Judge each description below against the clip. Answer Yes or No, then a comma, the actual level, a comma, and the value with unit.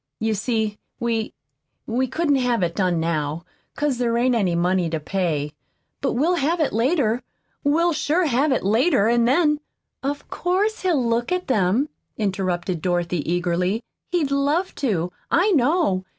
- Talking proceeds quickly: No, average, 160 wpm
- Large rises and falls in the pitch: Yes, wide, 8.1 semitones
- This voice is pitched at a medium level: No, high, 235 Hz